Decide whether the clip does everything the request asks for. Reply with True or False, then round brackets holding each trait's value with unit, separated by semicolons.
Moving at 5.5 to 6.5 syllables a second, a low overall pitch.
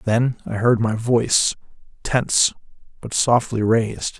False (4.3 syllables/s; 115 Hz)